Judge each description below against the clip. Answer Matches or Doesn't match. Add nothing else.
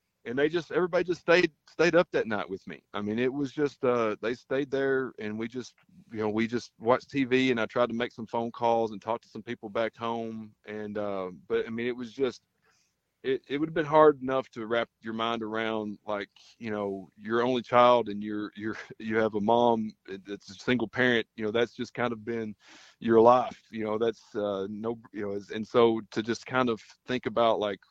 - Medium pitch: Doesn't match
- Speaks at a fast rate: Matches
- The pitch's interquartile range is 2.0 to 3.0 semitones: Matches